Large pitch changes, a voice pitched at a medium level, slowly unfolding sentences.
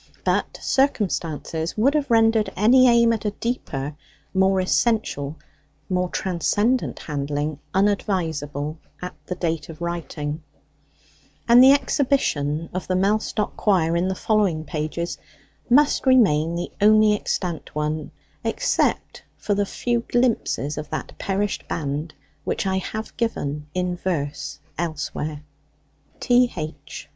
Yes: wide, 6.0 semitones; medium, 180 Hz; slow, 125 wpm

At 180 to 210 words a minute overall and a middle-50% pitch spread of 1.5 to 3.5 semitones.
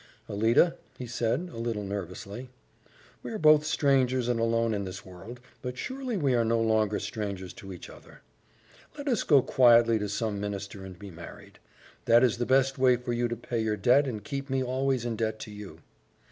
No: average, 200 wpm; average, 4.0 semitones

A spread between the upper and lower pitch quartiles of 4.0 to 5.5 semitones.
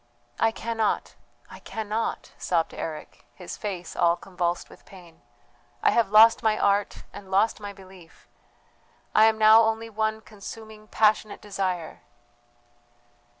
No: average, 2.8 semitones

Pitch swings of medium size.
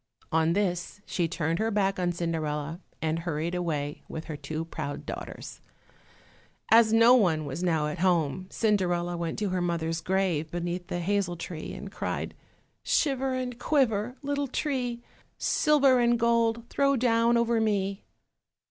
No: wide, 6.0 semitones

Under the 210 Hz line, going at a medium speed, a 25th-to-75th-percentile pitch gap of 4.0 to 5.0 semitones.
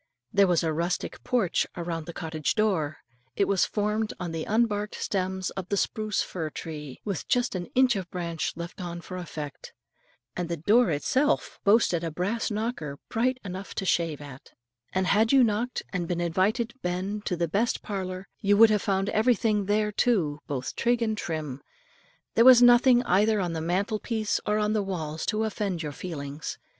Yes: high, 190 Hz; average, 190 wpm; average, 4.3 semitones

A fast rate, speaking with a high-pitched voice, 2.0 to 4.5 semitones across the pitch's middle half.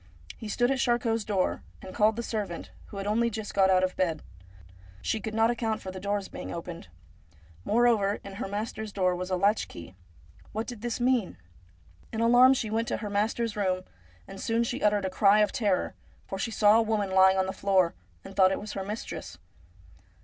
Yes: fast, 210 wpm; high, 210 Hz; average, 2.9 semitones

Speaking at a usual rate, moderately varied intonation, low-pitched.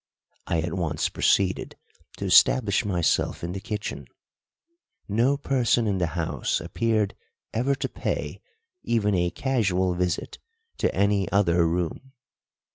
No: slow, 120 wpm; average, 4.6 semitones; low, 100 Hz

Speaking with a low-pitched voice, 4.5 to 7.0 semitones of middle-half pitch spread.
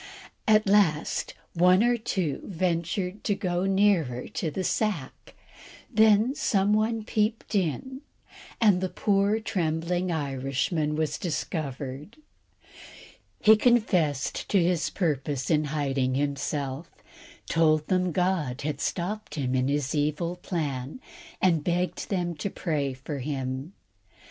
No: medium, 170 Hz; average, 5.3 semitones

